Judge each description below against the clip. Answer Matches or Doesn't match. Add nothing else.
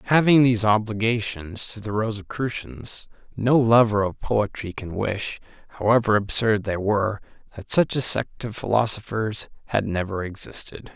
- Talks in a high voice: Doesn't match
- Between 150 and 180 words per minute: Doesn't match